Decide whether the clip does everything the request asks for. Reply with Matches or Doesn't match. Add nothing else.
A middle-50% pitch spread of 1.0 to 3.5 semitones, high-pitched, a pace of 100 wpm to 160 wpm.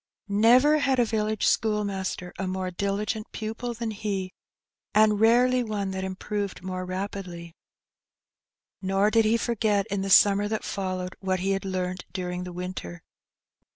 Matches